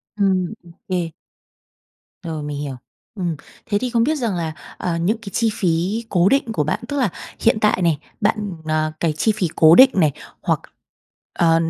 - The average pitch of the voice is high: No, medium, 180 Hz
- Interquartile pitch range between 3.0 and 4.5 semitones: No, average, 5.2 semitones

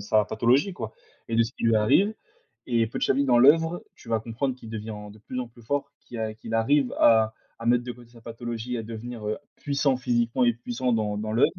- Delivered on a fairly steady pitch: Yes, narrow, 2.2 semitones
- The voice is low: Yes, low, 115 Hz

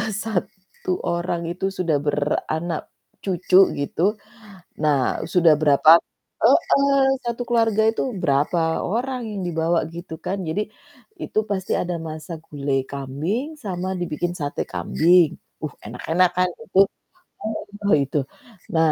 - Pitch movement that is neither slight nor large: Yes, average, 3.8 semitones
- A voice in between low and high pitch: Yes, medium, 175 Hz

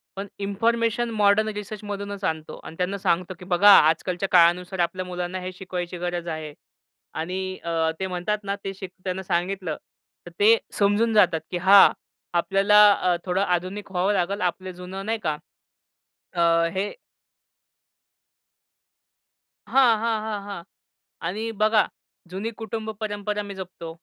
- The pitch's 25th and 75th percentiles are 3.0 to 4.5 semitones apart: No, narrow, 2.6 semitones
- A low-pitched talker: No, high, 190 Hz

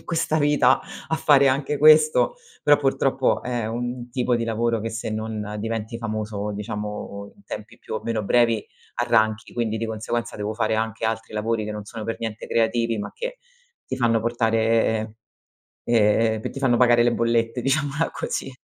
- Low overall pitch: Yes, low, 115 Hz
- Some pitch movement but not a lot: No, narrow, 2.2 semitones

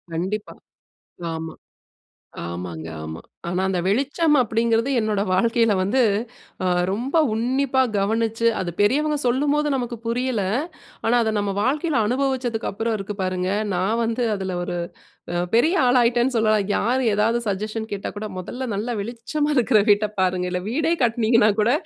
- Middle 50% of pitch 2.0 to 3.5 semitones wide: No, average, 3.9 semitones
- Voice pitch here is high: Yes, high, 225 Hz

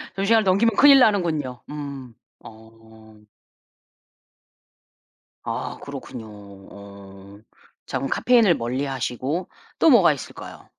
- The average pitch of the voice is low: Yes, low, 130 Hz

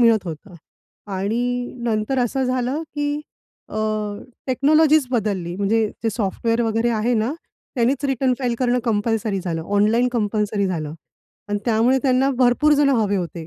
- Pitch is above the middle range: Yes, high, 230 Hz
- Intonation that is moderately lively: Yes, average, 3.8 semitones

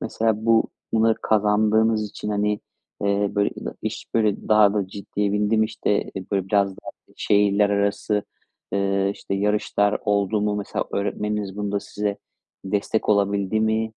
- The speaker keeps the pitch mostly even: Yes, narrow, 1.0 semitones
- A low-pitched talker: Yes, low, 105 Hz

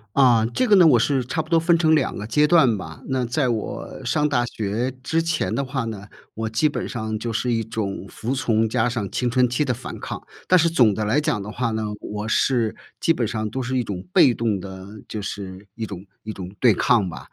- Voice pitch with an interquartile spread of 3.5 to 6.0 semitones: Yes, average, 4.1 semitones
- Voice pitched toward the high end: No, low, 115 Hz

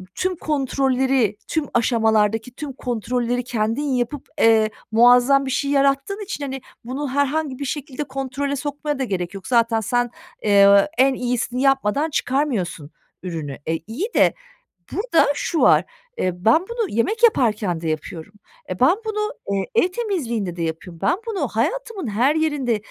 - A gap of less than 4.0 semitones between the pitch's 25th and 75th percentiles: No, average, 4.9 semitones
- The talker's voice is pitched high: Yes, very high, 255 Hz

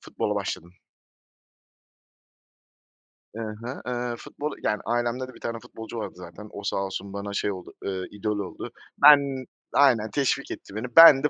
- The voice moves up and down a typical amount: Yes, average, 4.0 semitones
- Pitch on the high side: No, low, 115 Hz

